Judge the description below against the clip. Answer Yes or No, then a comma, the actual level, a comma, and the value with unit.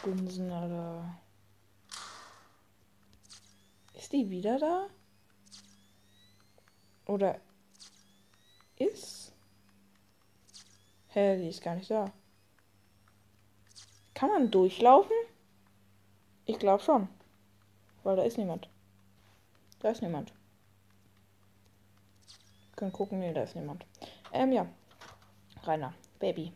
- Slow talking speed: Yes, slow, 85 wpm